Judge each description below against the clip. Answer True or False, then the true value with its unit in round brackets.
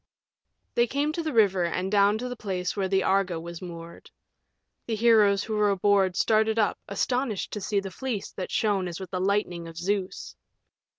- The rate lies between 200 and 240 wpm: False (190 wpm)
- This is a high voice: True (200 Hz)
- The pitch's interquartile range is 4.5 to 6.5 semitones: False (3.0 semitones)